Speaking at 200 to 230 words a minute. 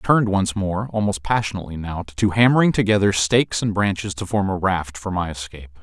Yes: fast, 205 wpm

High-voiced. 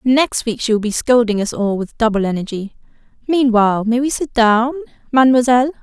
Yes: high, 235 Hz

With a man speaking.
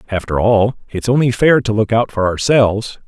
Yes: male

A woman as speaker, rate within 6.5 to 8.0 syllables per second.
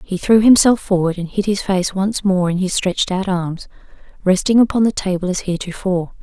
No: female; 5.6 syllables/s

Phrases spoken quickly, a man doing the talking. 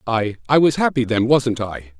No: average, 180 wpm; male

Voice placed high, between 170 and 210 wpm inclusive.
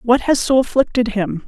Yes: high, 235 Hz; fast, 205 wpm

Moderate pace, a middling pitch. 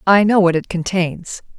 Yes: average, 190 wpm; medium, 180 Hz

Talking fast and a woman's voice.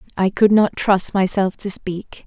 No: average, 185 wpm; female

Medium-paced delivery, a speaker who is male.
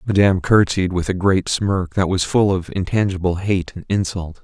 Yes: average, 190 wpm; male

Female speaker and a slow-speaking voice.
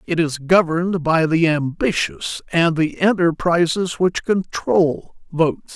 No: male; slow, 125 wpm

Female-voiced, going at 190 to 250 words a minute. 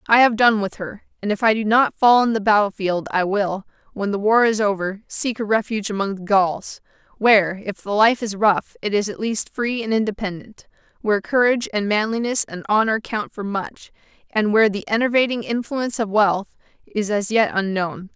Yes: female; average, 200 wpm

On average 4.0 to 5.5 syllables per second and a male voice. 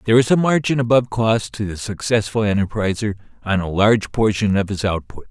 No: 6.0 syllables/s; male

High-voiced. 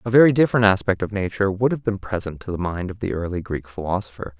No: very low, 95 Hz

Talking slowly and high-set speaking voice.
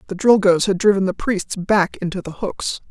No: fast, 205 wpm; high, 195 Hz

